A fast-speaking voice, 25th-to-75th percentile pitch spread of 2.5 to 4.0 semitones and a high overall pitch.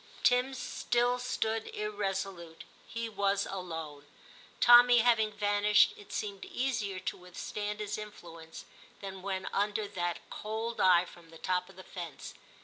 No: average, 140 wpm; average, 3.4 semitones; high, 205 Hz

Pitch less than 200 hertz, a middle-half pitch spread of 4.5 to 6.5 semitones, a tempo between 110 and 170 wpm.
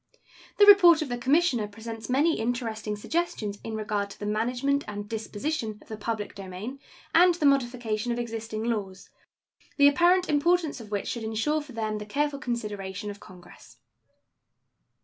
No: high, 230 Hz; average, 5.3 semitones; average, 160 wpm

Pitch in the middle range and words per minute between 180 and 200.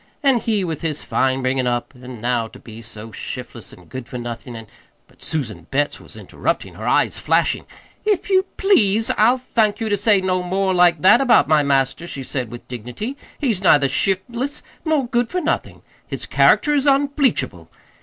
Yes: medium, 180 Hz; average, 190 wpm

